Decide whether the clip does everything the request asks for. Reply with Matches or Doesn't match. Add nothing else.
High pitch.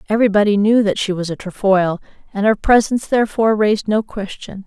Matches